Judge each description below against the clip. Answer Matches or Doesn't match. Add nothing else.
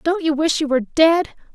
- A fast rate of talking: Matches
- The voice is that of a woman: Matches